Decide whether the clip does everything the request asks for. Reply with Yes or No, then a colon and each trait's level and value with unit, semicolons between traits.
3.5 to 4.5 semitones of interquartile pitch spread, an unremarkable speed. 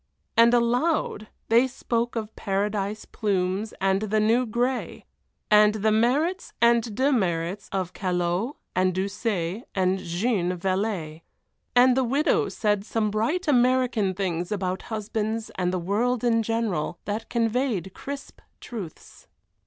No: average, 3.9 semitones; slow, 130 wpm